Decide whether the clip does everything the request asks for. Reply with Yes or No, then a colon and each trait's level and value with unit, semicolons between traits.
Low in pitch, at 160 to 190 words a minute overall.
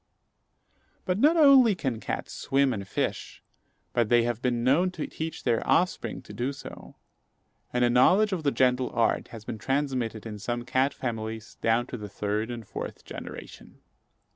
Yes: low, 125 Hz; average, 170 wpm